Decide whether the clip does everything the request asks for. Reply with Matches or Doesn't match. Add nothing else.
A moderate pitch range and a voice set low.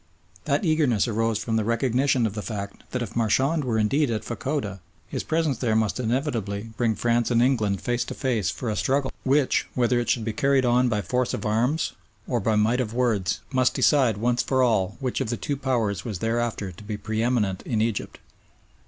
Matches